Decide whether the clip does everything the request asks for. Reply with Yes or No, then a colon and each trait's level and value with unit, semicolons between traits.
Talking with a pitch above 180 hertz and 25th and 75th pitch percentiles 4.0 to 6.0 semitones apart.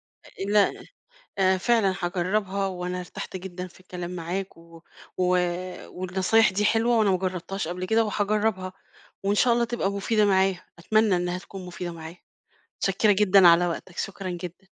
No: high, 190 Hz; narrow, 2.4 semitones